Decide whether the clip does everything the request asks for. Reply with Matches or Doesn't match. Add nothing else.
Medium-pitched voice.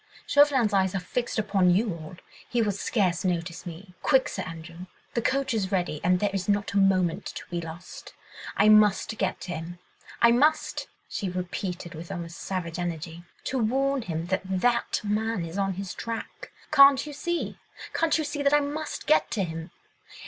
Doesn't match